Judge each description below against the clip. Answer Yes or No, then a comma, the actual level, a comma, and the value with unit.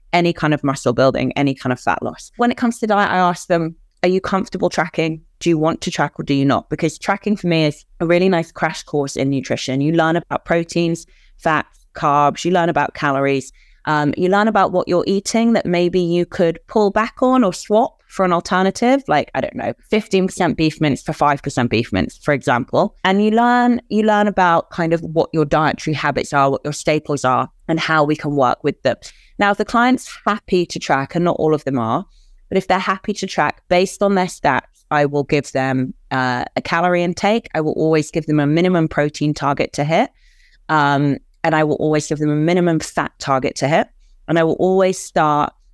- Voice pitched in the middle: Yes, medium, 165 Hz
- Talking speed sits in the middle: No, fast, 225 wpm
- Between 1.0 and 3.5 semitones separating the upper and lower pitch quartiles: No, average, 4.2 semitones